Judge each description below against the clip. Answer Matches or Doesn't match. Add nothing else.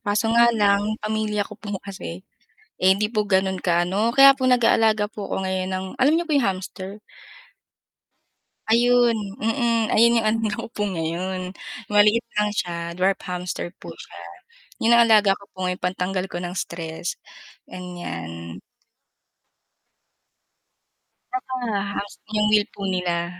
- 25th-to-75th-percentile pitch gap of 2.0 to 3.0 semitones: Doesn't match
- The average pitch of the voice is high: Matches